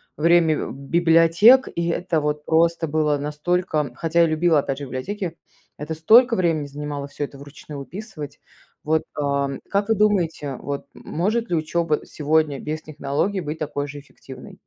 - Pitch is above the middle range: No, medium, 155 Hz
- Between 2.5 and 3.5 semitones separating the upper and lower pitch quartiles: Yes, average, 2.9 semitones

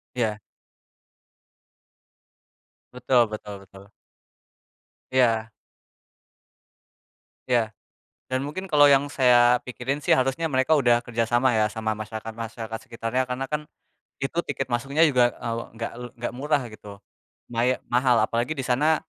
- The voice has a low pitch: Yes, low, 120 Hz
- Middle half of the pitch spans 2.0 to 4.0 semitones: Yes, average, 2.8 semitones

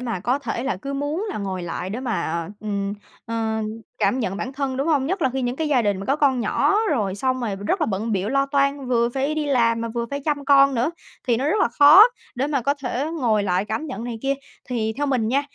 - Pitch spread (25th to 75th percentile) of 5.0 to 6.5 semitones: No, average, 4.1 semitones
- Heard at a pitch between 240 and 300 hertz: Yes, very high, 250 Hz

